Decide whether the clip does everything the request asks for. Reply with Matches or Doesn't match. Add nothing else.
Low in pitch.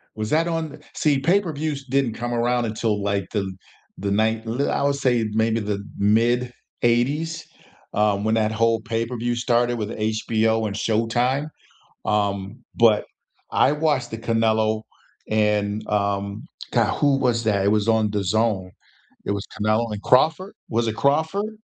Matches